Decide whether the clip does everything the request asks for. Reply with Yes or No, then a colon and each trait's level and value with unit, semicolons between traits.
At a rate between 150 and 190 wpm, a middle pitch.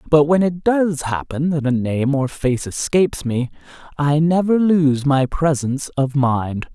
Yes: average, 170 wpm; medium, 145 Hz